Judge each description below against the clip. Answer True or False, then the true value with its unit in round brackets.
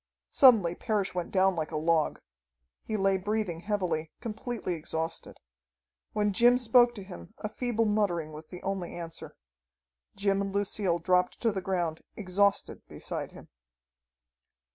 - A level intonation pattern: False (3.7 semitones)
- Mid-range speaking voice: False (195 Hz)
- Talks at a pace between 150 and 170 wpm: False (140 wpm)